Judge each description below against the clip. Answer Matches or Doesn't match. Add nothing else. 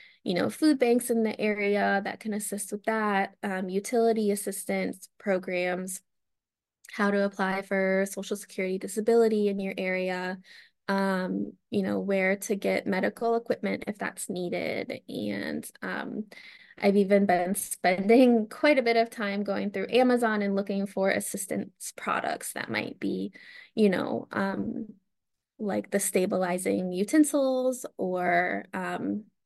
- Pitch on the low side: Doesn't match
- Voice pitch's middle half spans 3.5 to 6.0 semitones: Doesn't match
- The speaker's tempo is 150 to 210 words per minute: Doesn't match